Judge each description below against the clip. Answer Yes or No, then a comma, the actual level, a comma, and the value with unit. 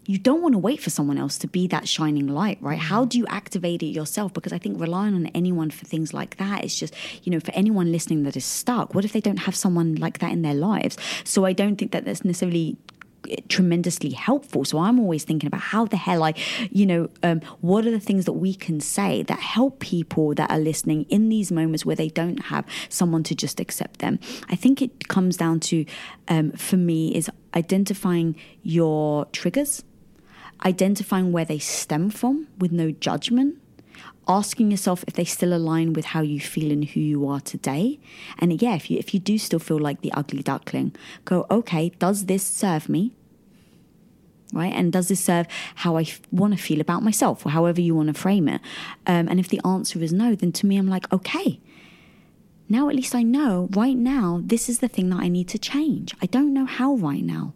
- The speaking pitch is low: No, medium, 185 Hz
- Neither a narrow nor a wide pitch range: Yes, average, 4.5 semitones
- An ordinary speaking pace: No, fast, 215 wpm